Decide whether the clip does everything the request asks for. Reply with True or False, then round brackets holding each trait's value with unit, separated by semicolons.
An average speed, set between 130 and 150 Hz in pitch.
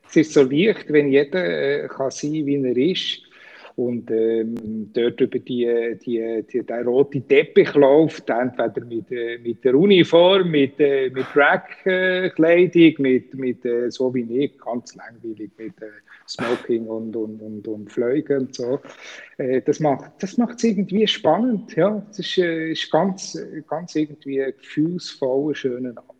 True (155 wpm; 140 Hz)